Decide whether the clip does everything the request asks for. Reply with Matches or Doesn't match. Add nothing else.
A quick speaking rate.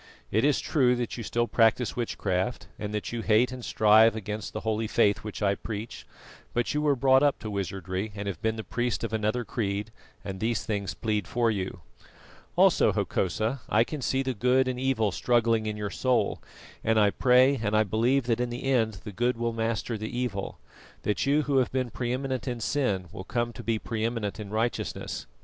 Matches